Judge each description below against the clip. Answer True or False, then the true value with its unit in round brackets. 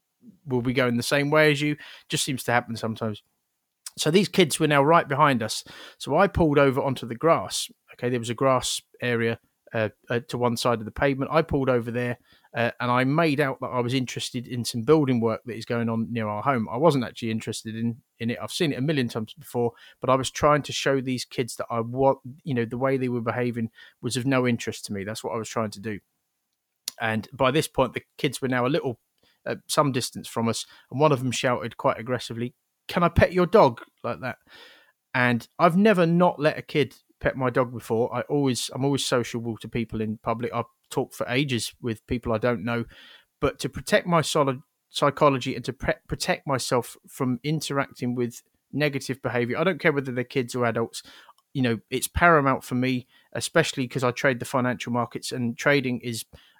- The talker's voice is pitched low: True (125 Hz)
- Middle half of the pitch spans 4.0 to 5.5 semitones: False (3.3 semitones)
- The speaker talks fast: True (220 wpm)